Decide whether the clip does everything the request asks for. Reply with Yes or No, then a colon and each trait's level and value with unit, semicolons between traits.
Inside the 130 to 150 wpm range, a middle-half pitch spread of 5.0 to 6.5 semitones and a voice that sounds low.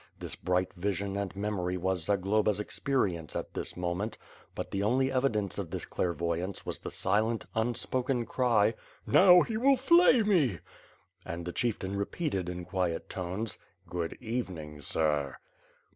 Yes: average, 145 wpm; wide, 5.4 semitones; low, 100 Hz